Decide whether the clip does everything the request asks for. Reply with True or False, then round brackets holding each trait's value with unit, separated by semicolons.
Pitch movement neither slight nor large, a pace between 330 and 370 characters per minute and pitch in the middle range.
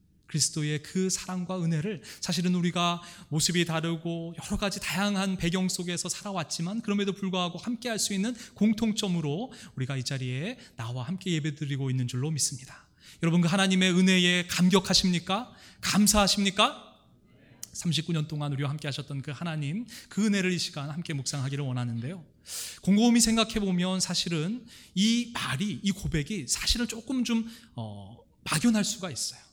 True (4.8 semitones; 355 characters per minute; 180 Hz)